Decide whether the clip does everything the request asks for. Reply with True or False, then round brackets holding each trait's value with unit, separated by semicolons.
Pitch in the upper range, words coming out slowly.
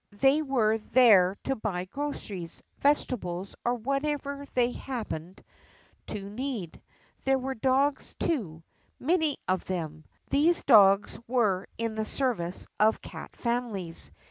True (230 Hz; 125 wpm)